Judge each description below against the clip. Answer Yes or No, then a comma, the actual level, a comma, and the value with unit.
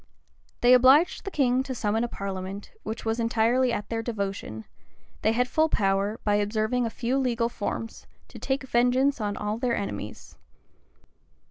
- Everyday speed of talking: Yes, average, 160 wpm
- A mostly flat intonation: No, average, 3.3 semitones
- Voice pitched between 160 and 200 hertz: No, high, 230 Hz